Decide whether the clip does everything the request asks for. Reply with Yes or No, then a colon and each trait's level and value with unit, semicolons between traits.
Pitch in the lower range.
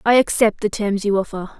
No: high, 210 Hz